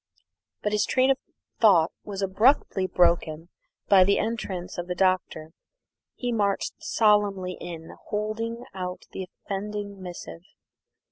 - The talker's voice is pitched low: No, high, 195 Hz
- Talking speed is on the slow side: Yes, slow, 125 wpm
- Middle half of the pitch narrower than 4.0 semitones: Yes, average, 2.8 semitones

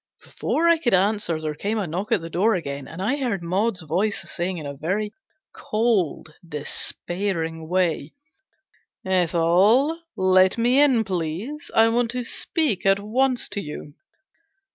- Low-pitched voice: No, high, 190 Hz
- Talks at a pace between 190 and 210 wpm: No, average, 155 wpm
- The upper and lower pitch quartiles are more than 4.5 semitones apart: Yes, wide, 5.4 semitones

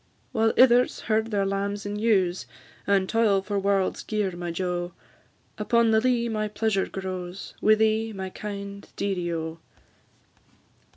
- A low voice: No, high, 200 Hz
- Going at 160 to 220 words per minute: No, average, 140 wpm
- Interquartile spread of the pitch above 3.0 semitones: No, narrow, 2.6 semitones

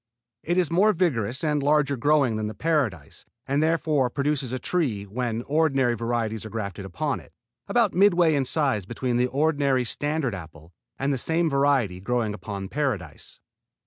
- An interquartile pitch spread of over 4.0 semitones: Yes, wide, 5.5 semitones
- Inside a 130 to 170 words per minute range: Yes, average, 165 wpm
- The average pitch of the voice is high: No, low, 130 Hz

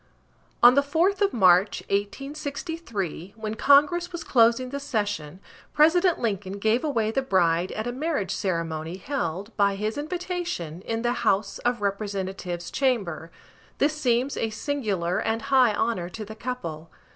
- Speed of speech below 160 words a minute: Yes, average, 145 wpm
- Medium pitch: No, high, 225 Hz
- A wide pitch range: Yes, wide, 6.6 semitones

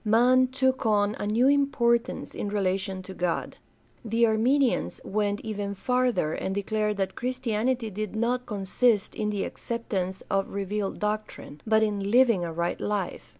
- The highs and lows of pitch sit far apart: No, average, 3.4 semitones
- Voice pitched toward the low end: No, high, 215 Hz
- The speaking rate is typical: Yes, average, 150 wpm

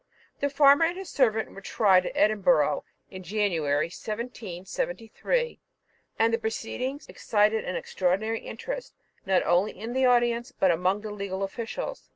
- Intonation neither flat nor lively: Yes, average, 4.8 semitones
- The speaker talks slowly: No, average, 145 wpm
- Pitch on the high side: Yes, high, 220 Hz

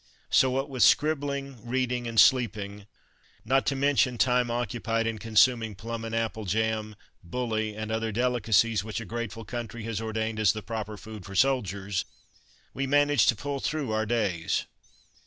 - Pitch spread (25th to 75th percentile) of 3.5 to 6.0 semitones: No, narrow, 2.6 semitones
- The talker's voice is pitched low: Yes, low, 115 Hz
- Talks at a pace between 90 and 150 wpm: No, average, 160 wpm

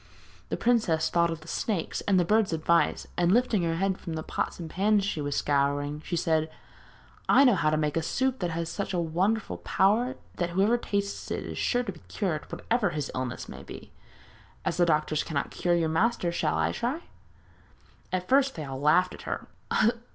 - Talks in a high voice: No, medium, 175 Hz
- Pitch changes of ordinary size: Yes, average, 4.8 semitones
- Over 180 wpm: Yes, fast, 205 wpm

